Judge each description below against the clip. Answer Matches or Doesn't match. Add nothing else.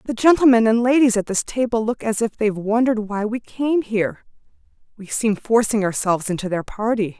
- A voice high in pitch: Matches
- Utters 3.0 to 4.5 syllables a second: Doesn't match